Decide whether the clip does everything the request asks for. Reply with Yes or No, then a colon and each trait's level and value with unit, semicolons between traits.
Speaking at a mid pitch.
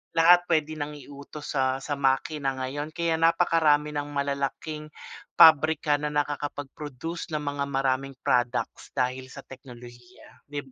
Yes: medium, 145 Hz